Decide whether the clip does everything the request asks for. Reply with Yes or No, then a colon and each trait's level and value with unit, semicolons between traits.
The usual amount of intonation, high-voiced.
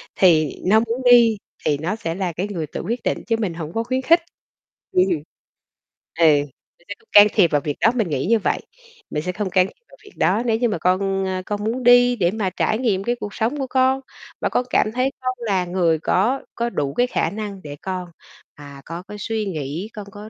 Yes: average, 4.8 semitones; high, 205 Hz